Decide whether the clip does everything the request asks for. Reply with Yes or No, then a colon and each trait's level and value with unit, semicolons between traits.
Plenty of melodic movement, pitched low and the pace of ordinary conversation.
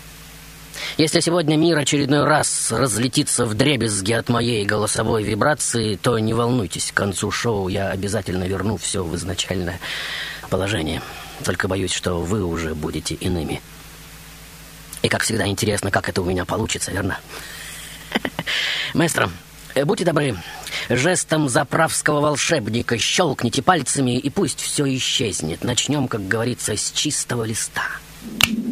Yes: wide, 6.7 semitones; low, 115 Hz; average, 125 wpm